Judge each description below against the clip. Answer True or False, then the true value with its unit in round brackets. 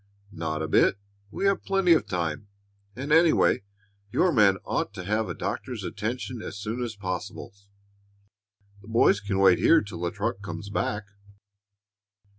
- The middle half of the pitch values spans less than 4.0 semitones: False (4.7 semitones)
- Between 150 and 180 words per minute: True (155 wpm)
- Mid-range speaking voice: False (105 Hz)